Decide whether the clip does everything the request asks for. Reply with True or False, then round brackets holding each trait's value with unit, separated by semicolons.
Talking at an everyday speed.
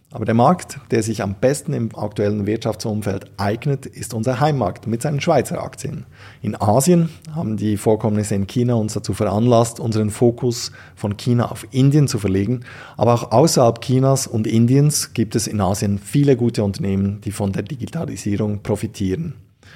True (165 wpm)